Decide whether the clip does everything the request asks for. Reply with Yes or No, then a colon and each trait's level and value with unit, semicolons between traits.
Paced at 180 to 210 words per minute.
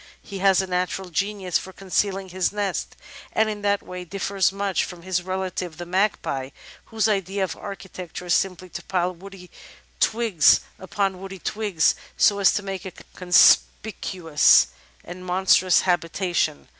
No: average, 155 wpm